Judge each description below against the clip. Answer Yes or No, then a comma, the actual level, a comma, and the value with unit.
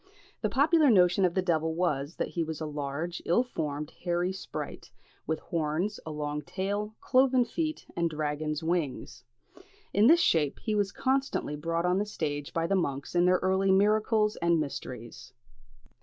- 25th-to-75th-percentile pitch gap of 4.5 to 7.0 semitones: Yes, average, 5.2 semitones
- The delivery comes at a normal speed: Yes, average, 170 wpm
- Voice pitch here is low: No, medium, 175 Hz